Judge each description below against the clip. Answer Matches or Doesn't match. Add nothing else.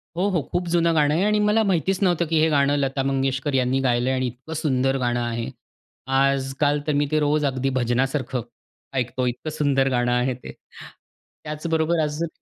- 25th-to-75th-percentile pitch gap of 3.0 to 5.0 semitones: Matches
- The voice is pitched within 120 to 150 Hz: Matches